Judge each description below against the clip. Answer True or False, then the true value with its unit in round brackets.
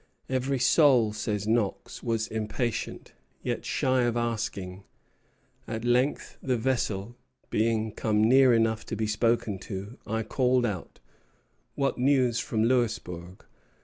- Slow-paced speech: True (125 wpm)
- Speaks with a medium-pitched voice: False (115 Hz)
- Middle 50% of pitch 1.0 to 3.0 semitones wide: True (2.7 semitones)